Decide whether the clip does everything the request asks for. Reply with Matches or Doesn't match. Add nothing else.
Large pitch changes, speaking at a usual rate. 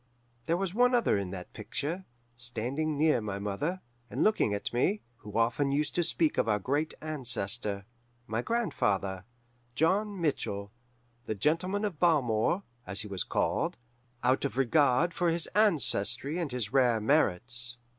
Matches